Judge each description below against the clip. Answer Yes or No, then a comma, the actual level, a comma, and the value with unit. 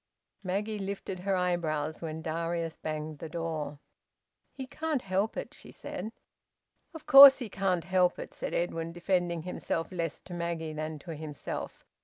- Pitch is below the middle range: No, medium, 170 Hz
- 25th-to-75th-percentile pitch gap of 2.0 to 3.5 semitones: Yes, average, 3.2 semitones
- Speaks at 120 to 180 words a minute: Yes, average, 155 wpm